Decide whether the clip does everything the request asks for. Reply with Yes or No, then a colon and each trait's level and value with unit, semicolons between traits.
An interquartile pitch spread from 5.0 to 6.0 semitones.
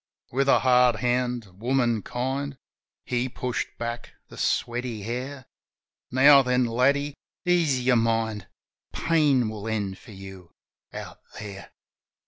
No: average, 2.8 semitones